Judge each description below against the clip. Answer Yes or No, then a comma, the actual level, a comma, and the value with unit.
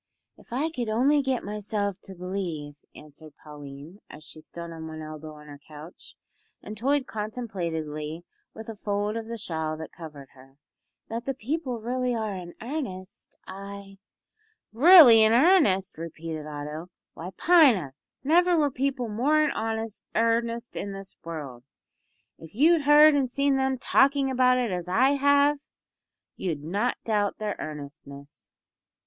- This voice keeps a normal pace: Yes, average, 150 wpm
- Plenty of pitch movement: Yes, wide, 8.2 semitones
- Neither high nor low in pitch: No, high, 210 Hz